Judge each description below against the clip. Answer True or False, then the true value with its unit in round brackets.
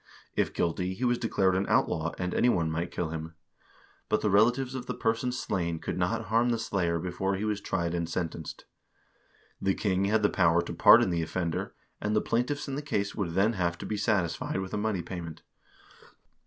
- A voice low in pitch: True (95 Hz)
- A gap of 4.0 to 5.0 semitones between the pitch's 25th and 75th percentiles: True (4.4 semitones)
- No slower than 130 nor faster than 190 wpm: False (200 wpm)